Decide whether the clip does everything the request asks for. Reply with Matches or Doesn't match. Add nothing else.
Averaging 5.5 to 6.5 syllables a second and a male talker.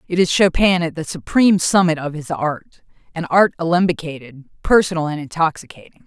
Doesn't match